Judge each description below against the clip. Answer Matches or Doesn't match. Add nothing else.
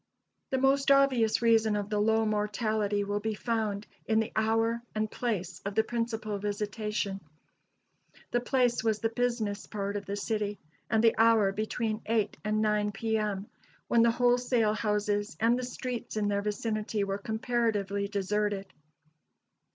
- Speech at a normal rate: Matches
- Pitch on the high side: Matches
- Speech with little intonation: Matches